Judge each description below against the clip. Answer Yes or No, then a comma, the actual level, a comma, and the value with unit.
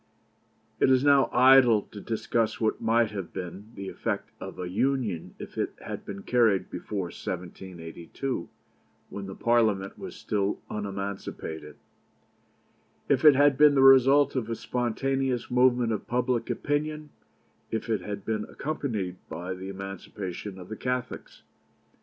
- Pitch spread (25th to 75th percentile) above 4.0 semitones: Yes, average, 4.8 semitones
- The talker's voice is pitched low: Yes, low, 110 Hz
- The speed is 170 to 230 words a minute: No, average, 140 wpm